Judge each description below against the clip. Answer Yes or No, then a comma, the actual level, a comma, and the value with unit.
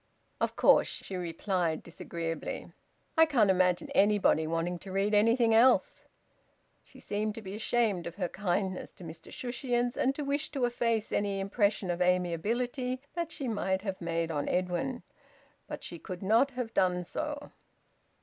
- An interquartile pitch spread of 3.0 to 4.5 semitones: No, average, 5.2 semitones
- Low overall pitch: No, high, 200 Hz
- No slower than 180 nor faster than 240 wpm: No, average, 160 wpm